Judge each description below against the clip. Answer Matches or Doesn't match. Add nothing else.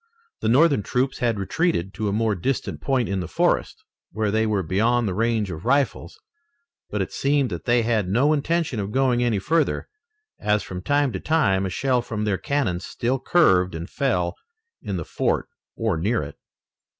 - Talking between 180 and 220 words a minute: Matches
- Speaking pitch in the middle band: Doesn't match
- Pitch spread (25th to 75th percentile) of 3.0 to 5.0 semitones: Doesn't match